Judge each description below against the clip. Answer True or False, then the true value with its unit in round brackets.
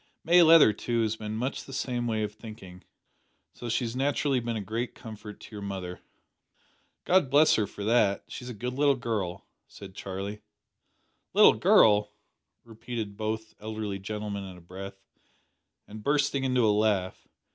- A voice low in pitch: True (110 Hz)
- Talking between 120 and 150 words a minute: False (165 wpm)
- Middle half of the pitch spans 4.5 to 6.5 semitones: False (3.3 semitones)